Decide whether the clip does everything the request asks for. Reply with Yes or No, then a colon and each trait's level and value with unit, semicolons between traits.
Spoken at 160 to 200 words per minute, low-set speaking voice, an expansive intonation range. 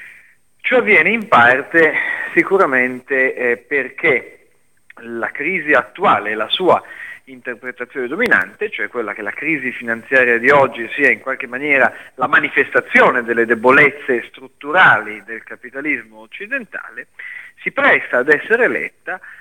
No: average, 120 wpm; low, 130 Hz; wide, 6.0 semitones